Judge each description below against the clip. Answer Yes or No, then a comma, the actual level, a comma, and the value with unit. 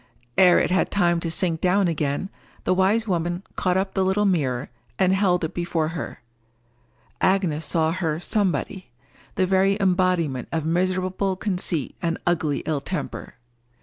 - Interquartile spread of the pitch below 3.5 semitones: Yes, average, 2.8 semitones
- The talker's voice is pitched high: No, medium, 180 Hz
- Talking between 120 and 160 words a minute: Yes, average, 150 wpm